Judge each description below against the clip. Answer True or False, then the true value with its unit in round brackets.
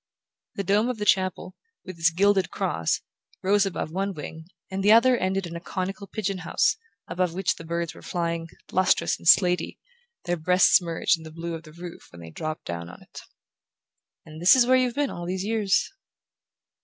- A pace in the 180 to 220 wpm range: True (195 wpm)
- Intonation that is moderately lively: True (3.0 semitones)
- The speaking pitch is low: False (180 Hz)